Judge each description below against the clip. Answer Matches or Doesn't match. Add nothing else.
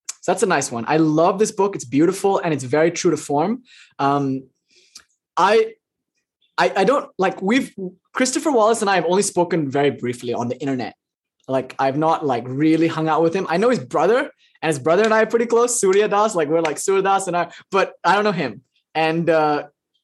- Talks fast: Matches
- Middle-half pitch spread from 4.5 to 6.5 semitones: Matches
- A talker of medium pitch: Matches